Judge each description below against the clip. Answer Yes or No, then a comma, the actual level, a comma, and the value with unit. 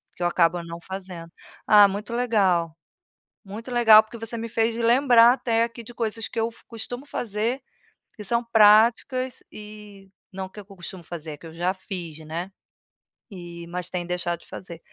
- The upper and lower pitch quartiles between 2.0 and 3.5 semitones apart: No, average, 4.6 semitones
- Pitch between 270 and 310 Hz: No, high, 210 Hz